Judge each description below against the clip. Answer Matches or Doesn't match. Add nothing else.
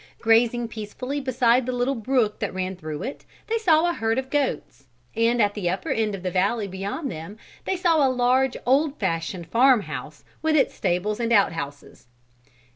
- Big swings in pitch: Matches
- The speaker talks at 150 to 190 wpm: Matches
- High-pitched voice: Matches